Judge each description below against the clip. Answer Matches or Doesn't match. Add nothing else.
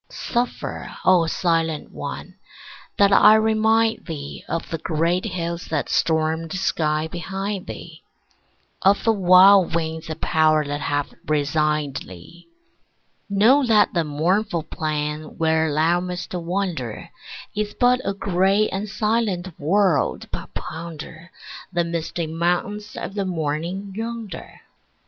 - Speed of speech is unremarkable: Doesn't match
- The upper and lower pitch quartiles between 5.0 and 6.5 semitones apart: Doesn't match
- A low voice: Doesn't match